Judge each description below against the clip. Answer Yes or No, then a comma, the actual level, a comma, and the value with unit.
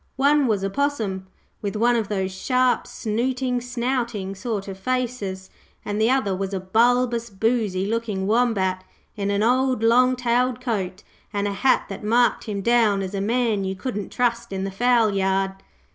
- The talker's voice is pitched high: Yes, high, 220 Hz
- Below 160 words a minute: No, average, 170 wpm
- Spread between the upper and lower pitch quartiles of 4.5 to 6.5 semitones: No, average, 4.1 semitones